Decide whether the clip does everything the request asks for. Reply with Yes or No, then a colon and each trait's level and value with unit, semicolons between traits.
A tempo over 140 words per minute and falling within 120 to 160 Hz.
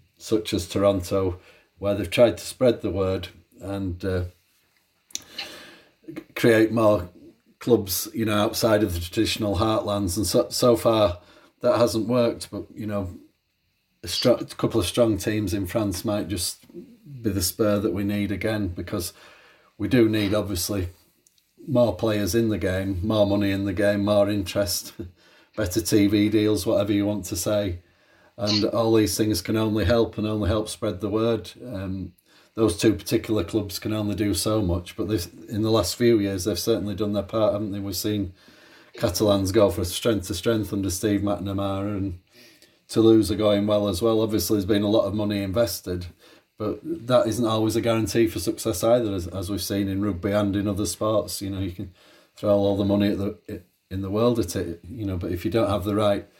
No: average, 195 wpm; low, 105 Hz